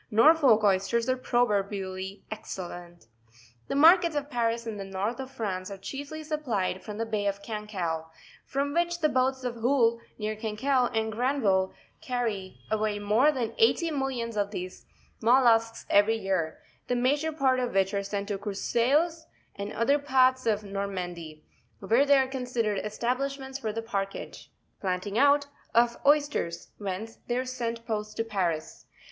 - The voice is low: No, high, 225 Hz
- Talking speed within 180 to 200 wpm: No, average, 160 wpm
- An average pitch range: Yes, average, 4.8 semitones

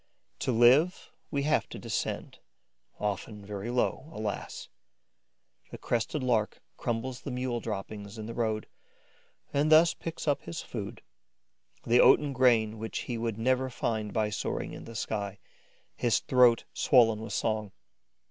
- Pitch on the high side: No, low, 115 Hz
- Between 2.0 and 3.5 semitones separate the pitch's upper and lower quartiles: Yes, average, 3.0 semitones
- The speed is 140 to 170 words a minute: Yes, average, 145 wpm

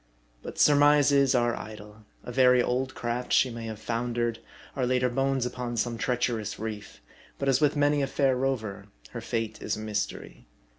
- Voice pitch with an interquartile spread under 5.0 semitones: Yes, average, 3.0 semitones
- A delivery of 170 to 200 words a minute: Yes, average, 180 wpm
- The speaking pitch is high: No, low, 125 Hz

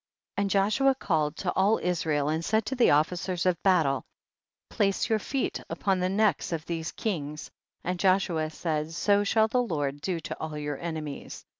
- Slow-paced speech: No, average, 180 wpm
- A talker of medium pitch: Yes, medium, 180 Hz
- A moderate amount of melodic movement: Yes, average, 4.5 semitones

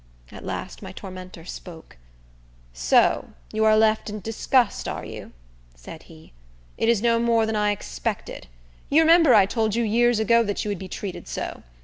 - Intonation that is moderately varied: Yes, average, 3.9 semitones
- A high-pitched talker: Yes, high, 215 Hz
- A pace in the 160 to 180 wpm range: Yes, average, 175 wpm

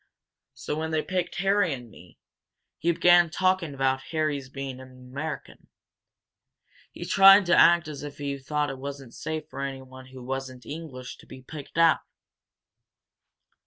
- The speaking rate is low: No, average, 155 wpm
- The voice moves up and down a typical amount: Yes, average, 3.9 semitones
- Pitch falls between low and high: Yes, medium, 145 Hz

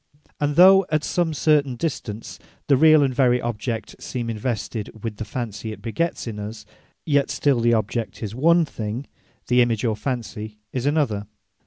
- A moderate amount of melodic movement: Yes, average, 4.7 semitones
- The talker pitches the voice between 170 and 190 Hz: No, low, 120 Hz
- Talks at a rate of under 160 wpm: No, average, 170 wpm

